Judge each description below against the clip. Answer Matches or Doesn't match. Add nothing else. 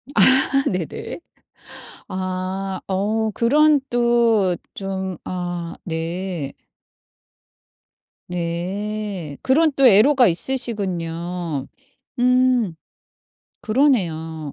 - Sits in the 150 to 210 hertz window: Matches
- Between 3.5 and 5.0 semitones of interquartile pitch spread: Doesn't match